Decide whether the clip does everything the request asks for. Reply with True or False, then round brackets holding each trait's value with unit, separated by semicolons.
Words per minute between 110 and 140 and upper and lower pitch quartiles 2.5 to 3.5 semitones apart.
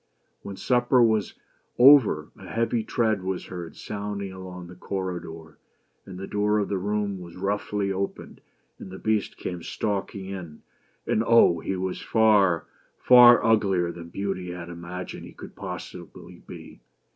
False (155 wpm; 2.9 semitones)